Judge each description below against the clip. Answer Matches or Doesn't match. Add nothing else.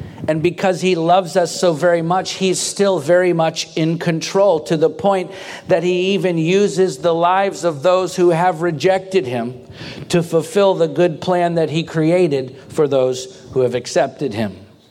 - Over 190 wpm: Doesn't match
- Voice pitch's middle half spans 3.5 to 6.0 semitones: Doesn't match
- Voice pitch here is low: Doesn't match